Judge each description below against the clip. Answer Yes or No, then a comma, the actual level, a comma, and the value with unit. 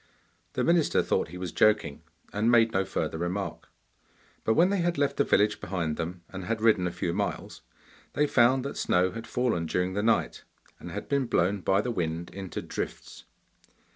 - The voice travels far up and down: No, average, 4.9 semitones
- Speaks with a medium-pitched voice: No, low, 100 Hz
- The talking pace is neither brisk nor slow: Yes, average, 190 wpm